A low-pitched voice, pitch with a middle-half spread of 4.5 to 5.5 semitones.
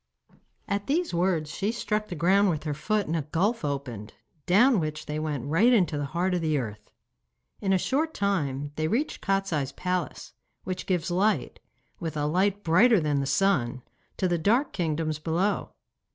No: medium, 175 Hz; average, 4.8 semitones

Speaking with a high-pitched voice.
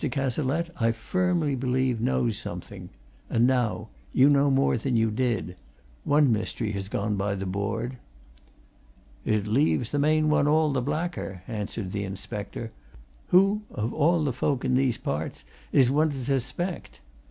No: low, 125 Hz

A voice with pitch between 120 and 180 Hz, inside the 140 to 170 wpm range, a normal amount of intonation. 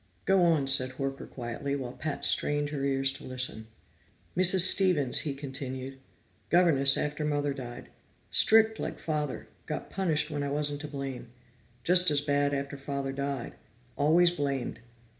No: medium, 140 Hz; average, 150 wpm; narrow, 2.0 semitones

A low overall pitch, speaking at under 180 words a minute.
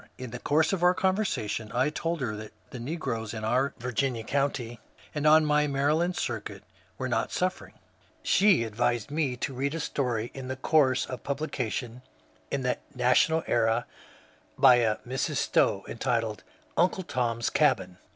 Yes: low, 130 Hz; average, 165 wpm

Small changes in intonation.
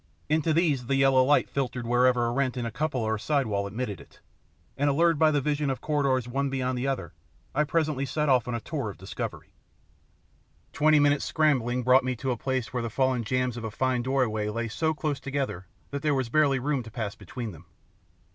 No: average, 3.2 semitones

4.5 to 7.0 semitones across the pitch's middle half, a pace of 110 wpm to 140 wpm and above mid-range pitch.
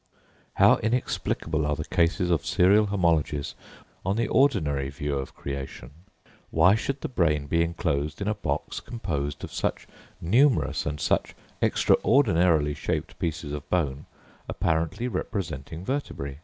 No: wide, 5.4 semitones; slow, 135 wpm; very low, 80 Hz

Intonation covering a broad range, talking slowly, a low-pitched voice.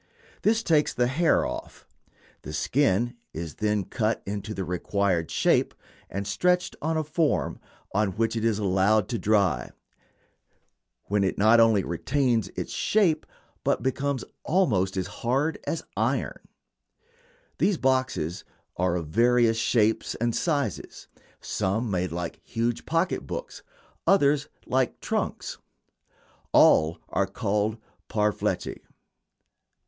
Yes: wide, 6.1 semitones; slow, 125 wpm; low, 110 Hz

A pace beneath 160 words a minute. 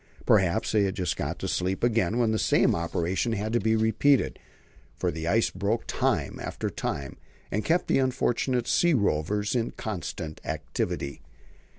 No: average, 165 wpm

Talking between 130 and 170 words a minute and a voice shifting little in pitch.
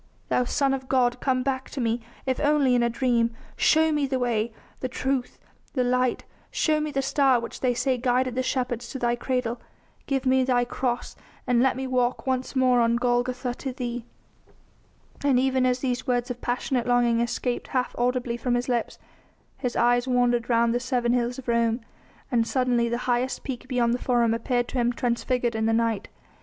No: average, 195 wpm; narrow, 1.4 semitones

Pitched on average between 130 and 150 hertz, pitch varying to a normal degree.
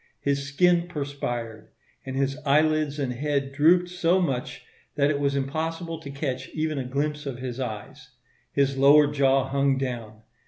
No: medium, 140 Hz; narrow, 2.2 semitones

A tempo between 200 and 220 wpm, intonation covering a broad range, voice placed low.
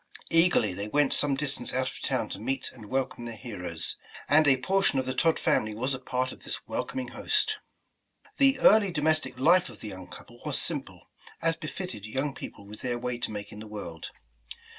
Yes: fast, 205 wpm; wide, 6.3 semitones; low, 130 Hz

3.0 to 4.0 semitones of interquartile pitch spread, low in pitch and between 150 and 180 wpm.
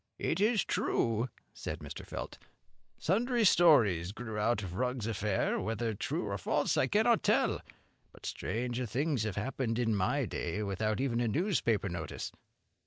No: average, 4.6 semitones; low, 115 Hz; average, 155 wpm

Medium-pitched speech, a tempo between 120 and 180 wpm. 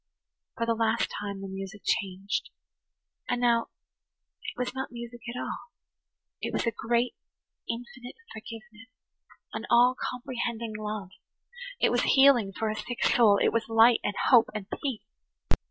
No: high, 230 Hz; average, 145 wpm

